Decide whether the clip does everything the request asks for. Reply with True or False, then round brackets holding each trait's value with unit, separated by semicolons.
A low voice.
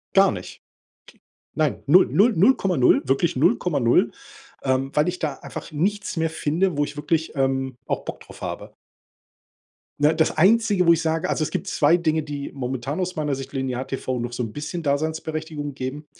False (150 Hz)